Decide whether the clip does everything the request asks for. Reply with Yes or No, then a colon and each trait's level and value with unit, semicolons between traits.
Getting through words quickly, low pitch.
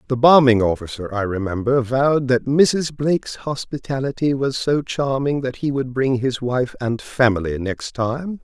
No: average, 165 wpm; low, 130 Hz